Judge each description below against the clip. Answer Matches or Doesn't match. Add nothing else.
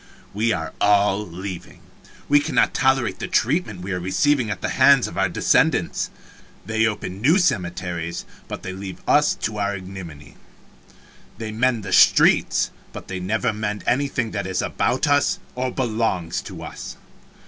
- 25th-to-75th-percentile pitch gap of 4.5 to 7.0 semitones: Matches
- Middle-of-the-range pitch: Doesn't match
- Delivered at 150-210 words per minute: Matches